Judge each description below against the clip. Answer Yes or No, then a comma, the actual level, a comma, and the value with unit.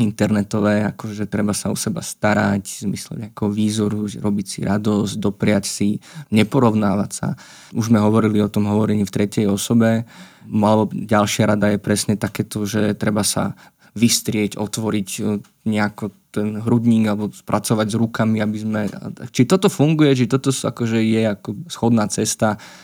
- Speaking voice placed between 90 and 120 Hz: Yes, low, 105 Hz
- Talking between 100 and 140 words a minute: No, average, 150 wpm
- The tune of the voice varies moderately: No, narrow, 1.5 semitones